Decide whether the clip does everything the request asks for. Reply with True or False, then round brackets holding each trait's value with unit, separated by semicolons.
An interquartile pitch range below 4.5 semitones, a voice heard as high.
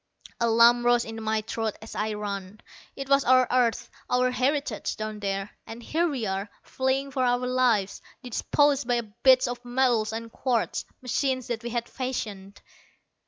True (2.8 semitones; 240 Hz)